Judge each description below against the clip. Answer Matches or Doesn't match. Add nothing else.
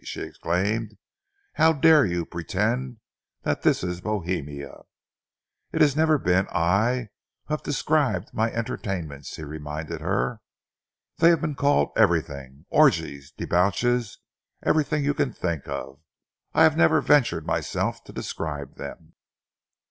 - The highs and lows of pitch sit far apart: Matches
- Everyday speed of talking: Doesn't match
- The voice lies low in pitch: Matches